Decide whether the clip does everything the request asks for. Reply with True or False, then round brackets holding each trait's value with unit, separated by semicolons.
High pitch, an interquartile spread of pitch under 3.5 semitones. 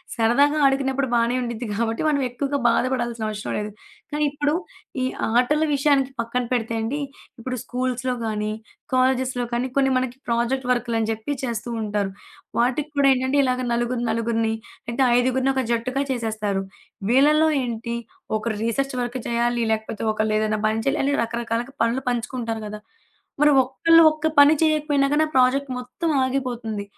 True (245 Hz; 2.8 semitones)